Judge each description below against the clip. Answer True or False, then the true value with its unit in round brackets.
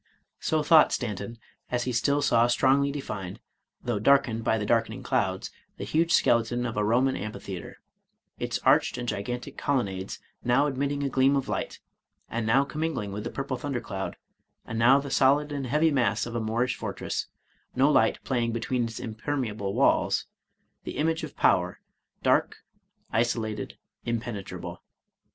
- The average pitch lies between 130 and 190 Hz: False (120 Hz)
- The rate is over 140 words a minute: True (160 wpm)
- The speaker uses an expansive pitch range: False (3.8 semitones)